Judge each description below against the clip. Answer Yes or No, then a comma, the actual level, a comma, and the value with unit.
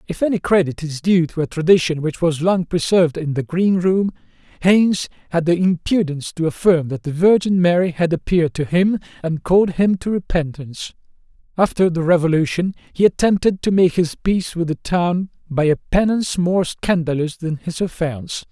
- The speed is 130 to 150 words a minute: No, average, 180 wpm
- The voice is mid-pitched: Yes, medium, 175 Hz